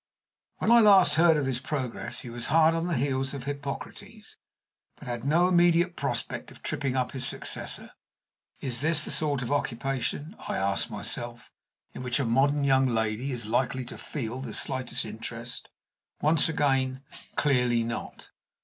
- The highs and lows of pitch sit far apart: No, average, 3.9 semitones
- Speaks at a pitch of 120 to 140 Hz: Yes, low, 135 Hz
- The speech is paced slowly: No, average, 165 wpm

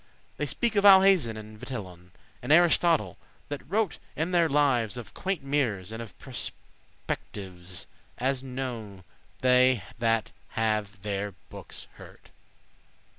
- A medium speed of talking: No, slow, 125 wpm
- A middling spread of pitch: No, wide, 6.0 semitones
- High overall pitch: No, low, 125 Hz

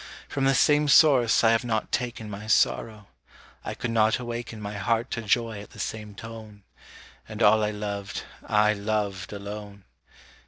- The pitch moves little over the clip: Yes, narrow, 2.0 semitones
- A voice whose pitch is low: Yes, low, 110 Hz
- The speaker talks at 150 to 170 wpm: Yes, average, 165 wpm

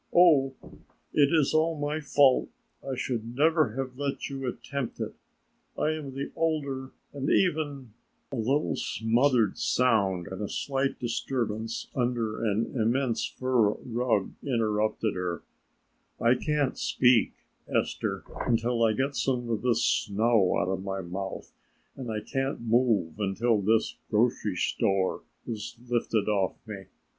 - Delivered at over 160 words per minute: No, average, 140 wpm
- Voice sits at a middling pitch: No, low, 120 Hz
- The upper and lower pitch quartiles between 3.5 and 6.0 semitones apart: Yes, average, 4.1 semitones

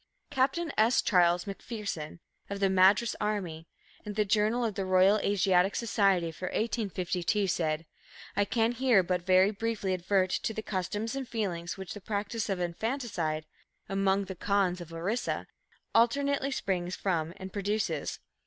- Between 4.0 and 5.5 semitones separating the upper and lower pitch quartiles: No, average, 3.3 semitones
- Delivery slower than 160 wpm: Yes, average, 150 wpm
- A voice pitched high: Yes, high, 195 Hz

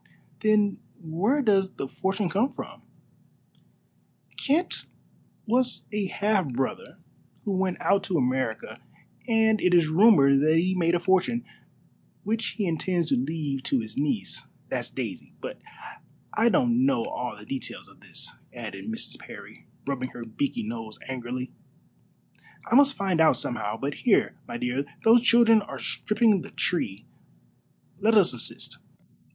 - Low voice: No, medium, 185 Hz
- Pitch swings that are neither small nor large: No, wide, 8.2 semitones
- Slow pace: No, average, 145 wpm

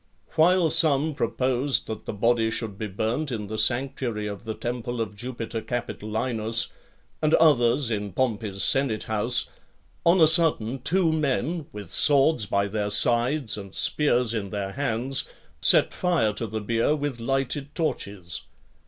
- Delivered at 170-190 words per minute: No, average, 150 wpm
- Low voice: Yes, low, 120 Hz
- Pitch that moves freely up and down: No, average, 4.6 semitones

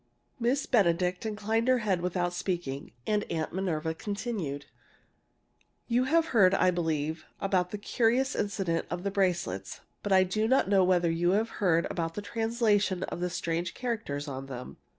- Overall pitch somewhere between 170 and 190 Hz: Yes, medium, 185 Hz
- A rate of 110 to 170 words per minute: Yes, average, 165 wpm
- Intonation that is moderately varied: Yes, average, 4.2 semitones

